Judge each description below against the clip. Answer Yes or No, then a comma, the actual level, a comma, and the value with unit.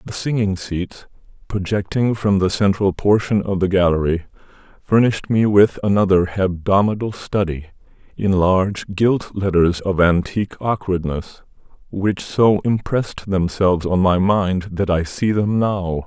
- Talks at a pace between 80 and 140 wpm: Yes, slow, 135 wpm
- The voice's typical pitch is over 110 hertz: No, very low, 95 Hz